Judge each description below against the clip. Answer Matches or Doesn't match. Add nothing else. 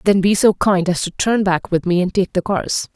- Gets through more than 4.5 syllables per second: Matches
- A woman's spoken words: Matches